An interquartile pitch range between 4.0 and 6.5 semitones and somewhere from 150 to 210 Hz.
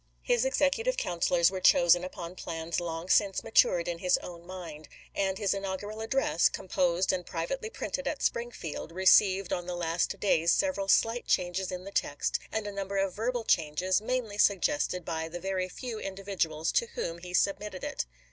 No: average, 3.3 semitones; medium, 185 Hz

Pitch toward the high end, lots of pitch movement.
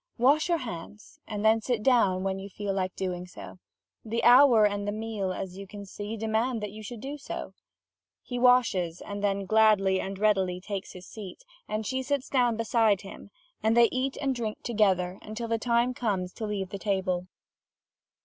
No: high, 215 Hz; average, 3.4 semitones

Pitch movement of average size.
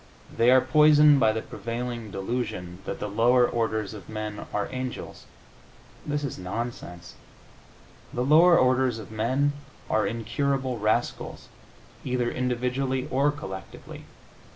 Yes: average, 3.3 semitones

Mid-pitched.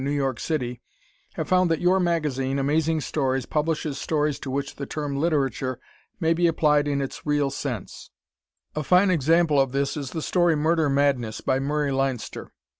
Yes: medium, 145 Hz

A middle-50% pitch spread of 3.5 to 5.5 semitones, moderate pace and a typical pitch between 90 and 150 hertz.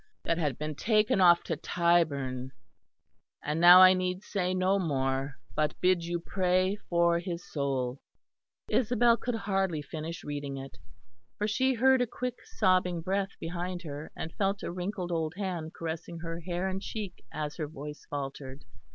No: average, 3.9 semitones; average, 160 wpm; medium, 175 Hz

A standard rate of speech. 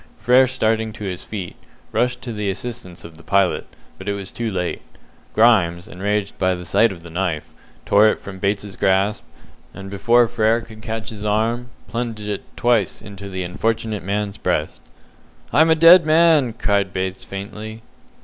Yes: average, 170 wpm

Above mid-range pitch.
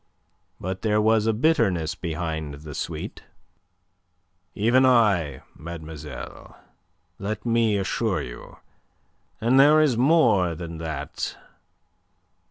No: low, 100 Hz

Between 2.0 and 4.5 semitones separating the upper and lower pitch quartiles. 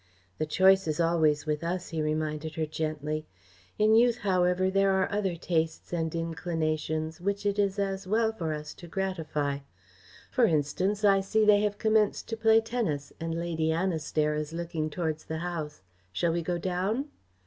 Yes: average, 3.9 semitones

